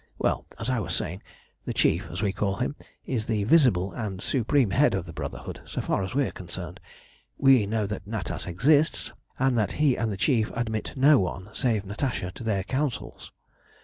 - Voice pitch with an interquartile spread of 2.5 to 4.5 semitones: No, wide, 5.4 semitones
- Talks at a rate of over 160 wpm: Yes, average, 195 wpm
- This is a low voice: Yes, low, 110 Hz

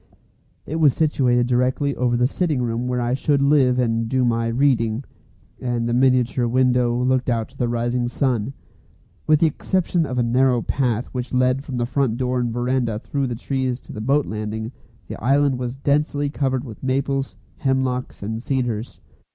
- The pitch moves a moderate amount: No, narrow, 2.1 semitones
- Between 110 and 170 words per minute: No, average, 180 wpm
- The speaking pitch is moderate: No, low, 125 Hz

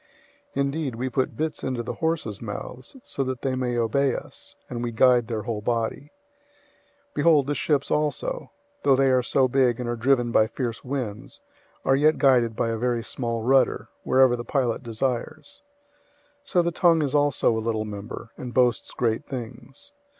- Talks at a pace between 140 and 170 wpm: No, average, 185 wpm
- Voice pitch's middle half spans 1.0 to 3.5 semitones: Yes, average, 3.0 semitones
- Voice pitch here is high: No, low, 125 Hz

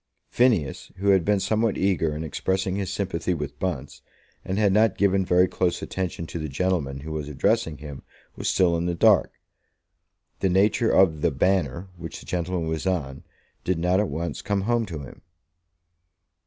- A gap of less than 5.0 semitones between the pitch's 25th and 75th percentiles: Yes, average, 3.4 semitones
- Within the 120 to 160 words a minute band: No, average, 180 wpm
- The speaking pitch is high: No, very low, 90 Hz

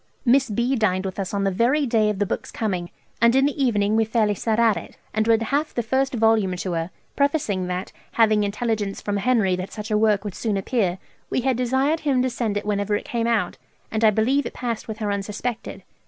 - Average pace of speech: No, fast, 230 wpm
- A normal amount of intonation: Yes, average, 3.2 semitones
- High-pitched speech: Yes, high, 220 Hz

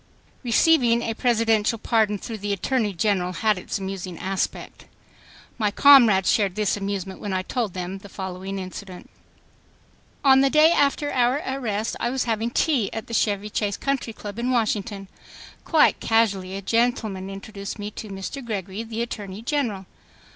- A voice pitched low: No, high, 215 Hz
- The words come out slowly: No, average, 160 wpm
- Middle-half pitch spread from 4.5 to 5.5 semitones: No, average, 3.4 semitones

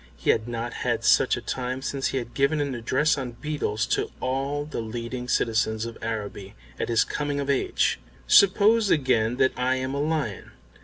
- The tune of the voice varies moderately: Yes, average, 3.6 semitones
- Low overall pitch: Yes, low, 130 Hz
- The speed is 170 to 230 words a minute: Yes, average, 190 wpm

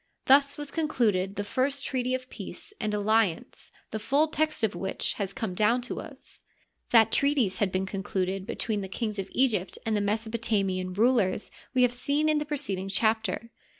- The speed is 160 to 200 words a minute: Yes, average, 180 wpm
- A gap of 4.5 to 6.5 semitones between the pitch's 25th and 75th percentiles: Yes, average, 4.8 semitones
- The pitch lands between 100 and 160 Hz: No, high, 220 Hz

